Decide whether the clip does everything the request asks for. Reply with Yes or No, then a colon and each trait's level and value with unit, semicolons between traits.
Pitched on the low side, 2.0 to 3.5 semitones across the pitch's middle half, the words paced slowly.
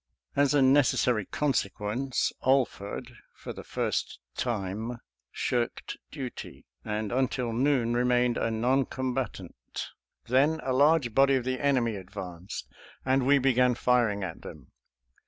Yes: low, 125 Hz; average, 3.2 semitones; slow, 125 wpm